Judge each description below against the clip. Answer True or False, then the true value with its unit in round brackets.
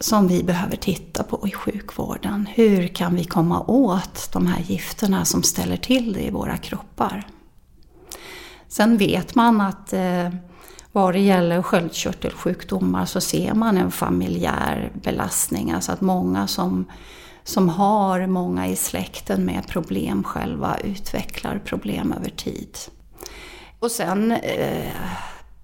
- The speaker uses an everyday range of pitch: True (3.8 semitones)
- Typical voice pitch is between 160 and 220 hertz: True (185 Hz)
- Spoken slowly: True (130 wpm)